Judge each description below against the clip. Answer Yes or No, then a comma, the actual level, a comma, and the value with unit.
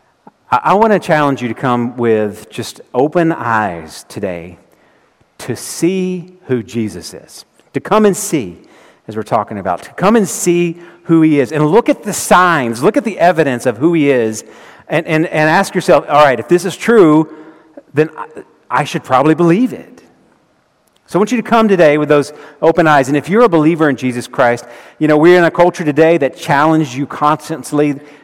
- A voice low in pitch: No, medium, 155 Hz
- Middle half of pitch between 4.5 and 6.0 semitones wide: No, average, 3.8 semitones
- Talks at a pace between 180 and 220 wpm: Yes, average, 195 wpm